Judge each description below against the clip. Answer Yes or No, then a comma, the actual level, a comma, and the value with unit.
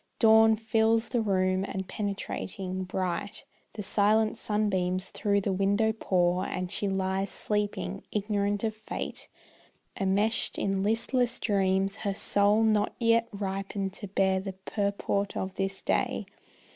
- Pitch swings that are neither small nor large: No, narrow, 2.2 semitones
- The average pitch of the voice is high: Yes, high, 200 Hz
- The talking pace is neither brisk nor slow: No, slow, 130 wpm